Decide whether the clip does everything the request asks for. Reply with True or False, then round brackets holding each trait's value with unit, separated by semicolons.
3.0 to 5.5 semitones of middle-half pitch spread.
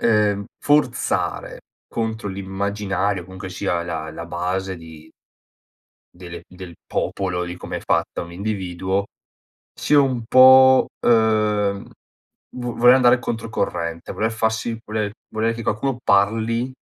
True (3.9 semitones)